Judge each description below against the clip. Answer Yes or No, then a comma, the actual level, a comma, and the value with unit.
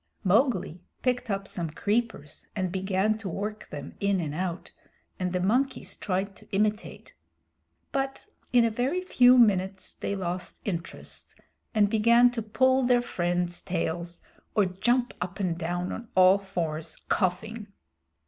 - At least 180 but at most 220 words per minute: No, average, 145 wpm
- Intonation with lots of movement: No, average, 4.3 semitones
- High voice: Yes, high, 195 Hz